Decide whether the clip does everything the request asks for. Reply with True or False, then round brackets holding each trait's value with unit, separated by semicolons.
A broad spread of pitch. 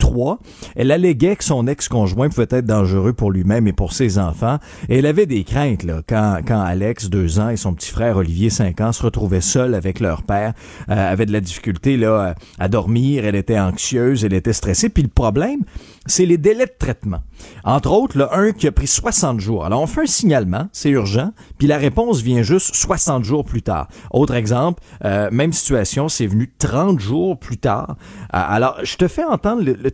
True (6.4 semitones)